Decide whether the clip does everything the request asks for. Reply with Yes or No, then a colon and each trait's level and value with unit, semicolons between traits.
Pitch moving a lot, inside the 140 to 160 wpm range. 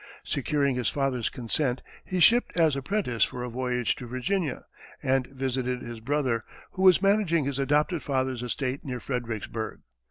No: average, 3.3 semitones; average, 155 wpm